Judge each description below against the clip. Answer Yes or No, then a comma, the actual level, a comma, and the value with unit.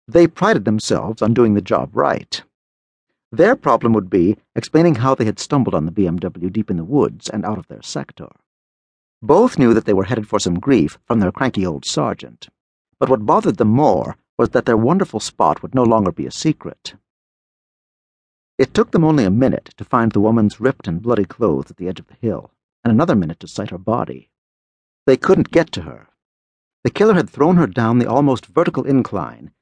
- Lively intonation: Yes, wide, 6.3 semitones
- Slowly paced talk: No, fast, 205 wpm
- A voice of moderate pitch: No, low, 110 Hz